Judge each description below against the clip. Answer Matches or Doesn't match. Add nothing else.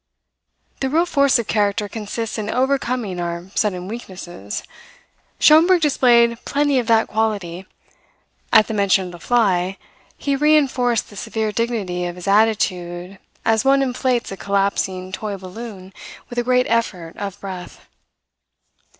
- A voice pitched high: Matches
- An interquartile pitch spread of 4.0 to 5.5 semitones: Matches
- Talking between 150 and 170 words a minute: Doesn't match